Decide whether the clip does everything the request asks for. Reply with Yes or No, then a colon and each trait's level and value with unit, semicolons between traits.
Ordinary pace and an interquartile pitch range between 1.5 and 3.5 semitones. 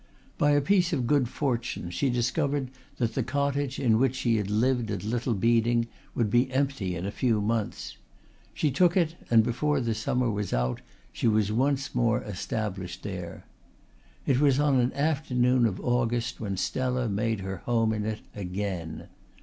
No: average, 175 wpm; average, 3.9 semitones